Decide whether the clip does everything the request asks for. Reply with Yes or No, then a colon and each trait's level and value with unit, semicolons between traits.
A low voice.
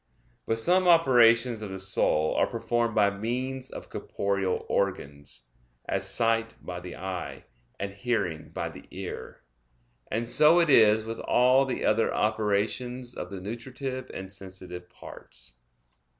Yes: low, 110 Hz